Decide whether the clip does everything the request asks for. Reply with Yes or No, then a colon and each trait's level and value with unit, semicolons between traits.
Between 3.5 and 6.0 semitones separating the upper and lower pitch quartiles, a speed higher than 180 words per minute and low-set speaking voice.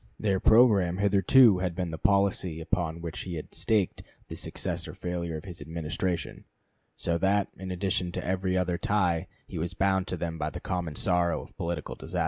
No: narrow, 2.4 semitones; average, 190 wpm; very low, 90 Hz